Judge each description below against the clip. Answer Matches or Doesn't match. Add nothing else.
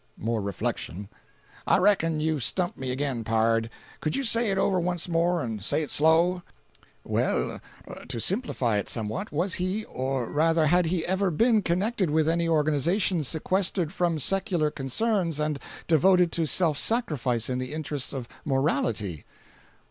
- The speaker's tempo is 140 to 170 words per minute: Matches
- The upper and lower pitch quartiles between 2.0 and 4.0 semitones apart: Doesn't match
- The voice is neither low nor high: Matches